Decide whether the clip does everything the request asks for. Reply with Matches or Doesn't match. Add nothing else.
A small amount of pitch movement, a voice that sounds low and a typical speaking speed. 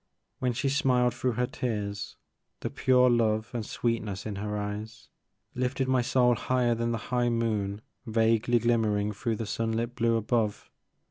Matches